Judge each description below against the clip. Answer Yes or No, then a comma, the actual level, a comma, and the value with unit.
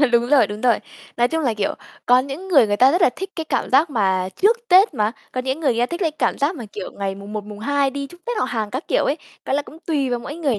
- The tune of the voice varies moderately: No, wide, 6.1 semitones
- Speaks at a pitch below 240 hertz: No, very high, 265 Hz